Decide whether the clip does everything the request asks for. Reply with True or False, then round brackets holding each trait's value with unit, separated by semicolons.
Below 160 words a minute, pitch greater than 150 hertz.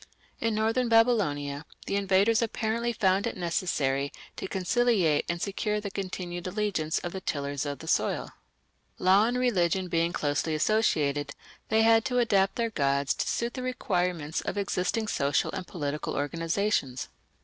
True (150 wpm; 190 Hz)